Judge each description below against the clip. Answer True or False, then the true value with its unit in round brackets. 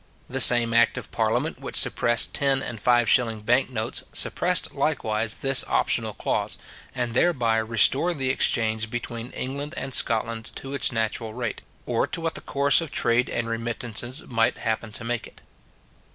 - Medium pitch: False (120 Hz)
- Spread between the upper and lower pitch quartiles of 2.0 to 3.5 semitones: True (2.8 semitones)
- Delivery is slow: False (165 wpm)